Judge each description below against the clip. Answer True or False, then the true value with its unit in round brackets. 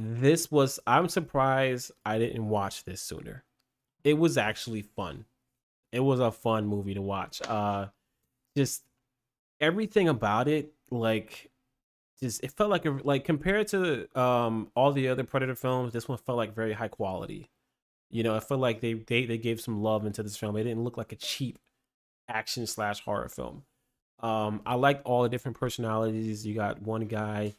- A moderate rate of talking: True (180 wpm)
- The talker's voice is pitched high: False (120 Hz)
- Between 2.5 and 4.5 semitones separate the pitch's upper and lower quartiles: True (3.4 semitones)